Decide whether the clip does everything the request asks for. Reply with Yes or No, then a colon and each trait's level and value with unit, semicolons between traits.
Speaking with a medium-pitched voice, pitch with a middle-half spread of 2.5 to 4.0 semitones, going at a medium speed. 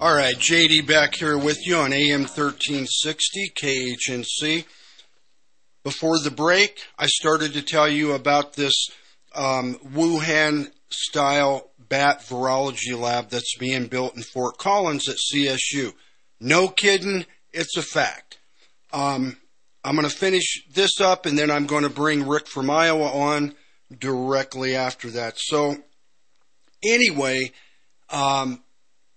No: medium, 145 Hz; average, 2.8 semitones; slow, 130 wpm